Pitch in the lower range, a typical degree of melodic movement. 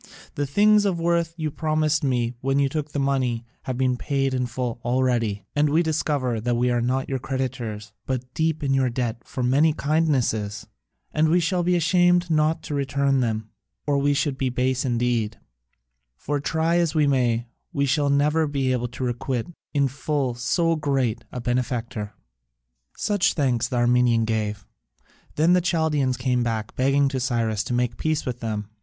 Yes: low, 130 Hz; average, 3.9 semitones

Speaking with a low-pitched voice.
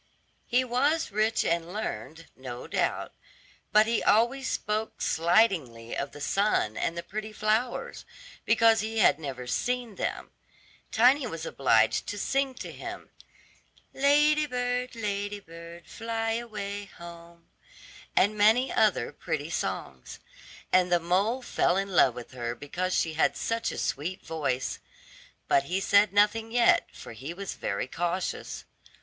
No: high, 200 Hz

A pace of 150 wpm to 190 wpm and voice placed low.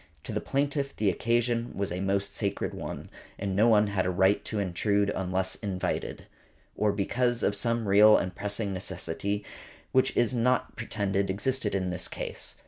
Yes: average, 175 wpm; low, 100 Hz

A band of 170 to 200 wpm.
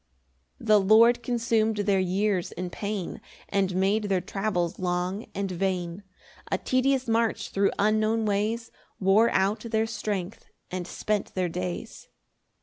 No: average, 140 wpm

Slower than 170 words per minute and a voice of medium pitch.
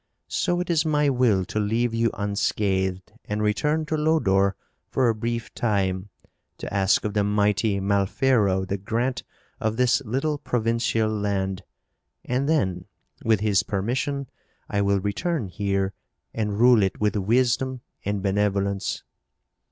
No: average, 140 wpm; low, 105 Hz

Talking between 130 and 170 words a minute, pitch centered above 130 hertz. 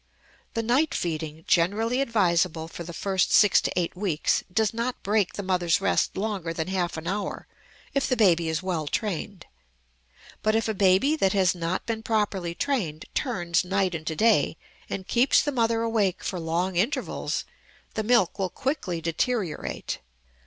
Yes: average, 165 wpm; high, 190 Hz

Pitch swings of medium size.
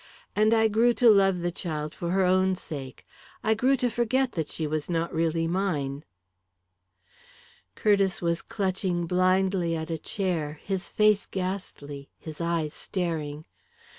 Yes: average, 3.8 semitones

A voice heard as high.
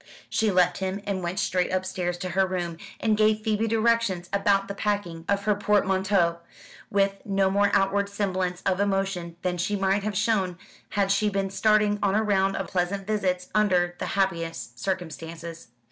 Yes: high, 195 Hz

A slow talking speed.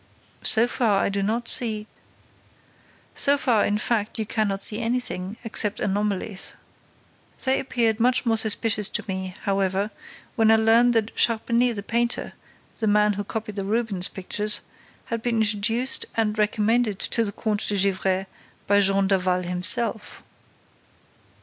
No: average, 145 wpm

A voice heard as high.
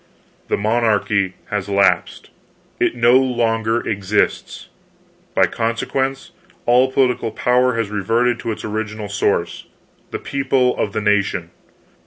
No: low, 115 Hz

